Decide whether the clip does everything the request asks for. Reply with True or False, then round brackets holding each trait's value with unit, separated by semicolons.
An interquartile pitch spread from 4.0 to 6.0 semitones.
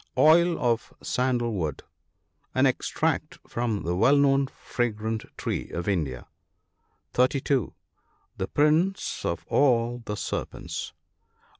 True (4.9 semitones)